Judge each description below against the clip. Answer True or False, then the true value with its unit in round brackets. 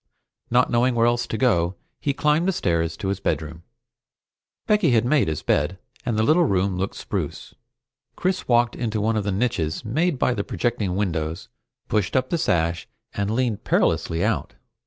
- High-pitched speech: False (110 Hz)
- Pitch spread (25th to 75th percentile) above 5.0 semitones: True (5.6 semitones)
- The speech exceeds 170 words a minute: True (180 wpm)